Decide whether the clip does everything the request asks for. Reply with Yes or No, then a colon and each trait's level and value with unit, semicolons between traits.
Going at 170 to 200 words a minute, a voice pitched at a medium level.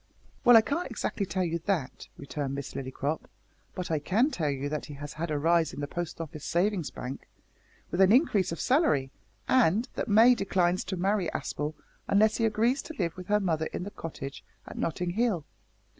Yes: average, 195 wpm; medium, 175 Hz